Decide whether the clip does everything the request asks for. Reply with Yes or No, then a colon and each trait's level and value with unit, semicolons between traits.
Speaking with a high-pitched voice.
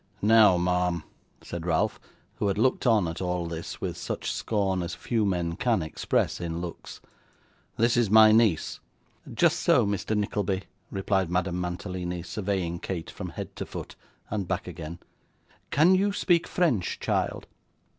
No: very low, 95 Hz